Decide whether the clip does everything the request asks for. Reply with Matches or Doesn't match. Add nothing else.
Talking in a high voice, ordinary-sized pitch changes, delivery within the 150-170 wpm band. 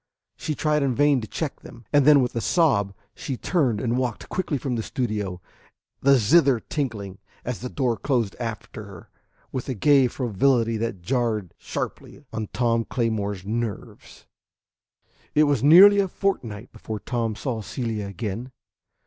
Doesn't match